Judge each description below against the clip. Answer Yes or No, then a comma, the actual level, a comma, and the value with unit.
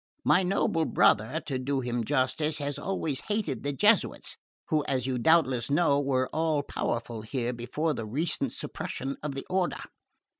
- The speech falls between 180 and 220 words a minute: No, average, 160 wpm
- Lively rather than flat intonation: No, average, 3.8 semitones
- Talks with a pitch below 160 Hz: Yes, medium, 140 Hz